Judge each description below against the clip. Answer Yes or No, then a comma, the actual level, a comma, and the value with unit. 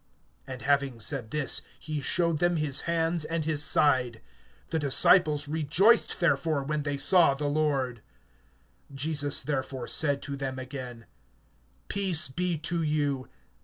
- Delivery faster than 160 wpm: No, slow, 135 wpm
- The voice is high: No, medium, 145 Hz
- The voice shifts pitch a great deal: No, average, 2.9 semitones